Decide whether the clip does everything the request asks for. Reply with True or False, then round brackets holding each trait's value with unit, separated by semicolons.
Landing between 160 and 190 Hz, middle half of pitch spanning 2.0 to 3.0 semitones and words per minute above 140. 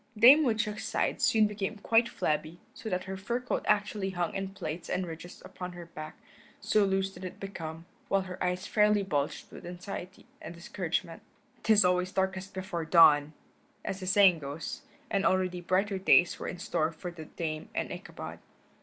True (185 Hz; 2.6 semitones; 180 wpm)